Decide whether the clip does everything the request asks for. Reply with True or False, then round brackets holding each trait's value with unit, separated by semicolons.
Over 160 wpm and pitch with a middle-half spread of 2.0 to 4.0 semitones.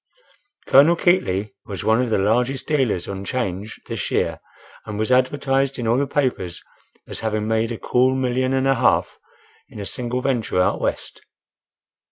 True (170 wpm; 3.7 semitones)